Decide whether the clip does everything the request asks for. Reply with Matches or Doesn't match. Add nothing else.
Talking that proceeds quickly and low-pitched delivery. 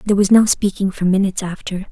Doesn't match